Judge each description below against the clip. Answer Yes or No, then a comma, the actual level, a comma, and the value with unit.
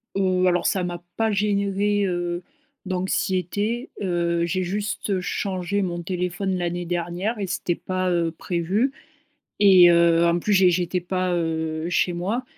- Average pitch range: No, narrow, 2.2 semitones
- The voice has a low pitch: No, medium, 180 Hz